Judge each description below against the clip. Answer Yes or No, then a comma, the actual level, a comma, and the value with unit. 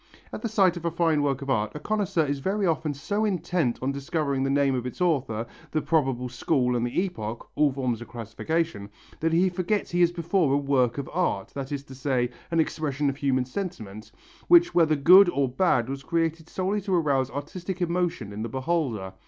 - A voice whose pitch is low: No, medium, 145 Hz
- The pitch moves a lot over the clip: No, average, 5.0 semitones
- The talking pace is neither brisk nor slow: No, fast, 210 wpm